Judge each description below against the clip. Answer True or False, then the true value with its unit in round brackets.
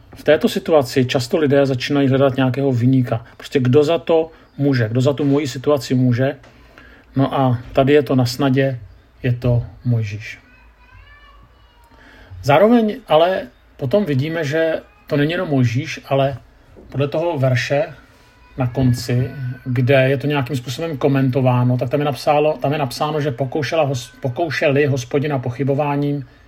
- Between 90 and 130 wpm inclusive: False (145 wpm)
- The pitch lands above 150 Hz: False (140 Hz)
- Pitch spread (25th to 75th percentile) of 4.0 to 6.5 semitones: False (2.5 semitones)